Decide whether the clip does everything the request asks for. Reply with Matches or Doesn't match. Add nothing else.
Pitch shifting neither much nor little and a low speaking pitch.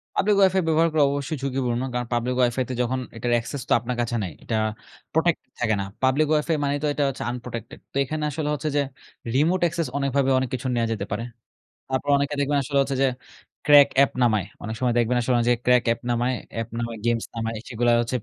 Matches